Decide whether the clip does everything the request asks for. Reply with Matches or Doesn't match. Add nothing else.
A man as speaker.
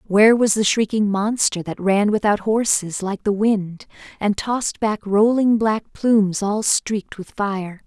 Doesn't match